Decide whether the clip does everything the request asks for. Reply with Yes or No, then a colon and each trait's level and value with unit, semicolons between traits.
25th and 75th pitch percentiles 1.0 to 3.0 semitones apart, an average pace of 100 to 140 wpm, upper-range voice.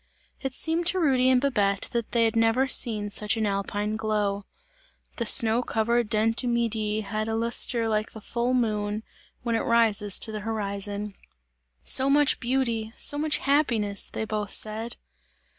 No: narrow, 2.4 semitones; average, 165 wpm; high, 225 Hz